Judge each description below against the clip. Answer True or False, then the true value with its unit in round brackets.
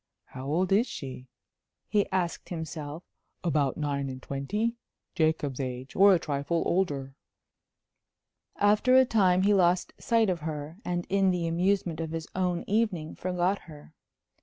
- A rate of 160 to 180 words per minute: False (145 wpm)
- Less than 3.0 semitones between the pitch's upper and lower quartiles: False (4.6 semitones)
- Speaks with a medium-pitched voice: True (170 Hz)